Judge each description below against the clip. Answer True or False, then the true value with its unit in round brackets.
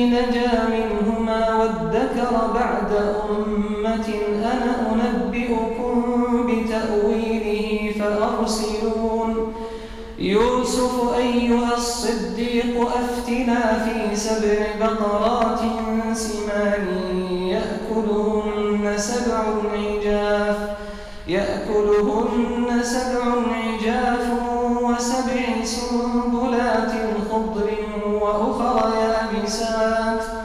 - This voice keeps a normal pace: False (55 wpm)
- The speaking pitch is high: True (225 Hz)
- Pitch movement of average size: False (2.0 semitones)